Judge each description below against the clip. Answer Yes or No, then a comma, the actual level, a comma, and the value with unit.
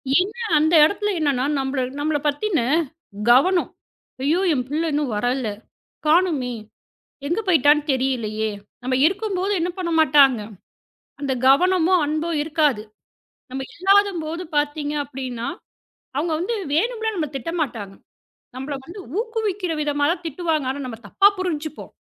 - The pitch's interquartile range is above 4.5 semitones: Yes, average, 5.1 semitones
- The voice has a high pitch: Yes, very high, 310 Hz